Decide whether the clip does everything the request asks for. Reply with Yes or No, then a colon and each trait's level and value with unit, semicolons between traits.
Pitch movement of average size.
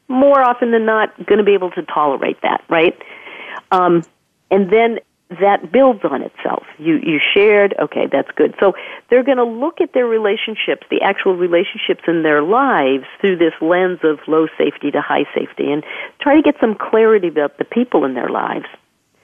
No: wide, 6.4 semitones